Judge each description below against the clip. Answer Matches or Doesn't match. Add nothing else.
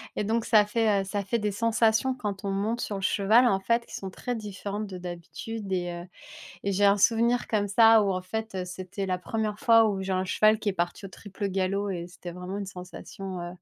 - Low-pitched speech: Doesn't match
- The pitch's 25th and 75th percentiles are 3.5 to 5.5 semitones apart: Doesn't match